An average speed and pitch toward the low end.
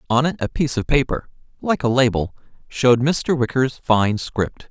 Yes: average, 180 wpm; low, 125 Hz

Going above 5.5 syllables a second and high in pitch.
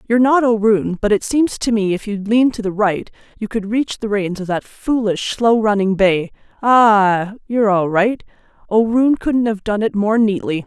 No: 4.6 syllables/s; high, 215 Hz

